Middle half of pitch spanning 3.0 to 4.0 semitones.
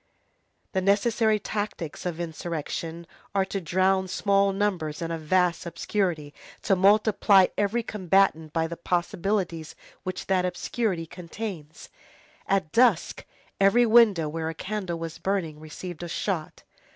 Yes: average, 3.3 semitones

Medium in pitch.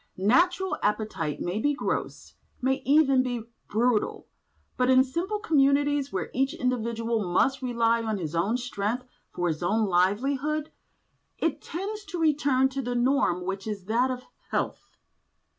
No: very high, 250 Hz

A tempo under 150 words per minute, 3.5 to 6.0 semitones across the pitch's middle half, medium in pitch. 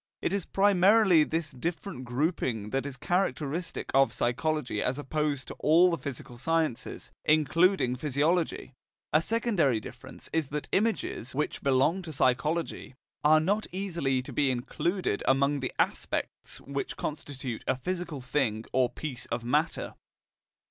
Yes: average, 140 wpm; average, 4.6 semitones; medium, 150 Hz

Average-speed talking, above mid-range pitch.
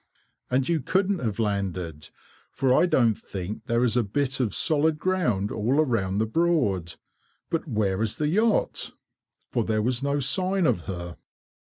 No: average, 165 wpm; low, 120 Hz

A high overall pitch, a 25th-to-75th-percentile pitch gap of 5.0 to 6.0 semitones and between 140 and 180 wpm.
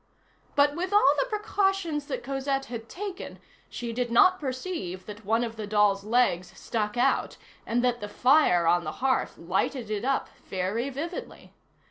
Yes: high, 245 Hz; wide, 5.5 semitones; average, 165 wpm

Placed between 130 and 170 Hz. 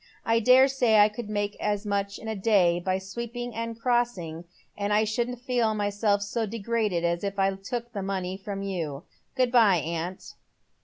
No: high, 205 Hz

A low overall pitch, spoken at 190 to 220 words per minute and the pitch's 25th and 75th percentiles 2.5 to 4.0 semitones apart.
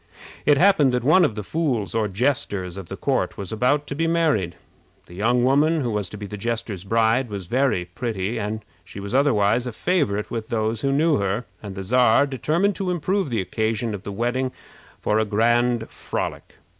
No: low, 115 Hz; average, 200 wpm; average, 5.1 semitones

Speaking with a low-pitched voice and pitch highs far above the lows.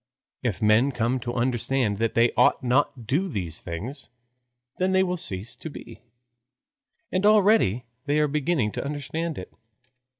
Yes: low, 130 Hz; wide, 5.7 semitones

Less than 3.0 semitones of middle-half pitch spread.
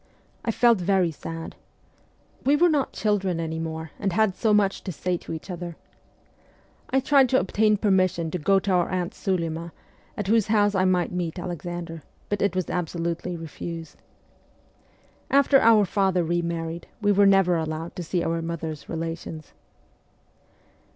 No: average, 3.5 semitones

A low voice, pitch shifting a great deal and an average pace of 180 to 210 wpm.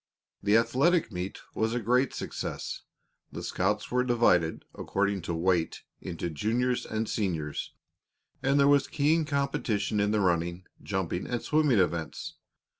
No: low, 110 Hz; wide, 5.9 semitones; average, 140 wpm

